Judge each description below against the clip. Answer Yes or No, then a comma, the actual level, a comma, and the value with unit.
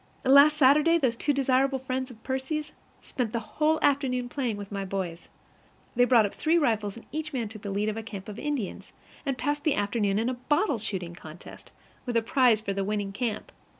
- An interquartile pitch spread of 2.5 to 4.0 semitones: No, average, 5.1 semitones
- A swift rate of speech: Yes, fast, 210 wpm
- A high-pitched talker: Yes, high, 245 Hz